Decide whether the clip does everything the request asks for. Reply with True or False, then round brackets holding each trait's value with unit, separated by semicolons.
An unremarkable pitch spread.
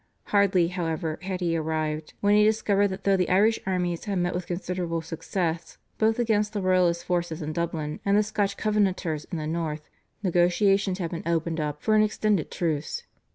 True (3.5 semitones)